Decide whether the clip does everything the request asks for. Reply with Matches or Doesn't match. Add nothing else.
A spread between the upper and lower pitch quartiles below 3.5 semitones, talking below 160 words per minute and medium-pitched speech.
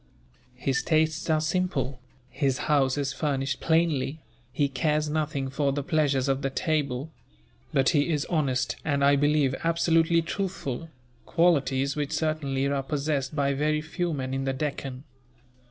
Matches